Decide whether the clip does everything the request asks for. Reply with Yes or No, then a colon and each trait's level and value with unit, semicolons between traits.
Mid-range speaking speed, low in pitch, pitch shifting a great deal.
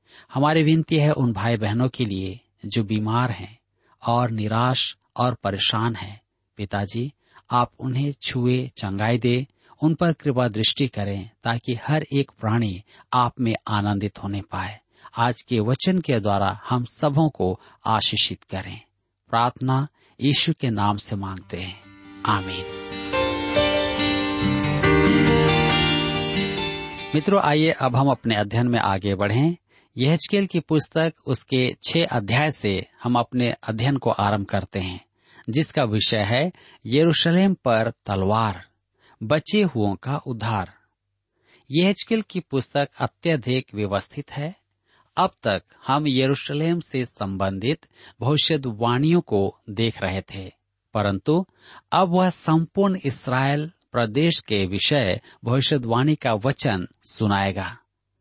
Yes: average, 120 wpm; low, 115 Hz; wide, 6.1 semitones